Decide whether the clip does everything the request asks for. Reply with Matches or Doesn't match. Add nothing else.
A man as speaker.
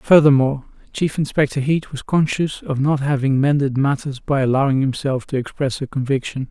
Matches